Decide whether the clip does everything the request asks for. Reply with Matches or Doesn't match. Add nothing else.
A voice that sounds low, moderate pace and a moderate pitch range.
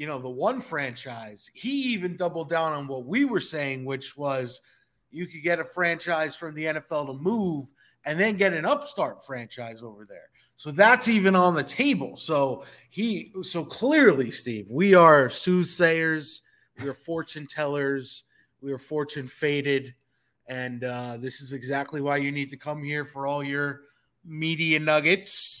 Doesn't match